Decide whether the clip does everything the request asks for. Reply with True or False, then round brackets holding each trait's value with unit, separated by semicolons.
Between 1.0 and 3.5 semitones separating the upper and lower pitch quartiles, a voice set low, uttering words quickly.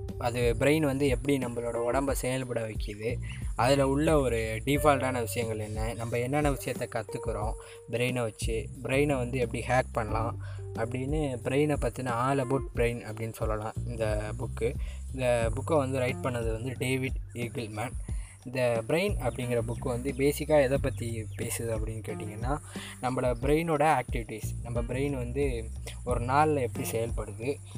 True (3.0 semitones; 120 Hz; 140 wpm)